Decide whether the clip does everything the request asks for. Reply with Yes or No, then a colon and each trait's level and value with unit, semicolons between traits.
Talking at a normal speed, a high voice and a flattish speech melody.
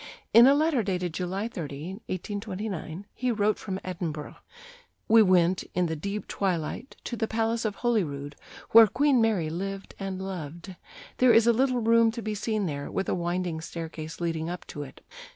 No: average, 175 wpm; high, 195 Hz; average, 4.8 semitones